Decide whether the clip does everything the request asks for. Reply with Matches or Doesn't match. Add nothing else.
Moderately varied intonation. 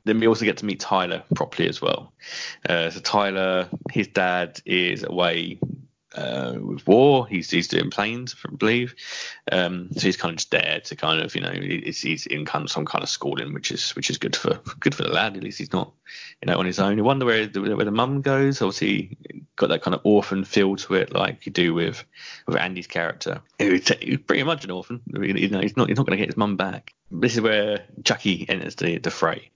Matches